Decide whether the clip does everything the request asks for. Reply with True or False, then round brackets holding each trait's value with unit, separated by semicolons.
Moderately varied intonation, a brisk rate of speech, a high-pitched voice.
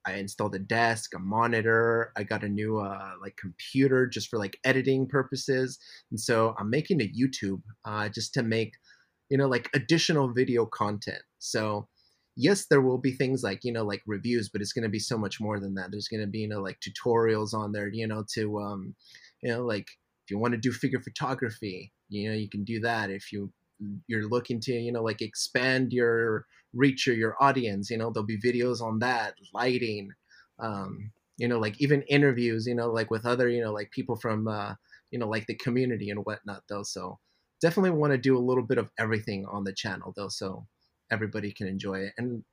False (3.3 semitones; 215 wpm; 110 Hz)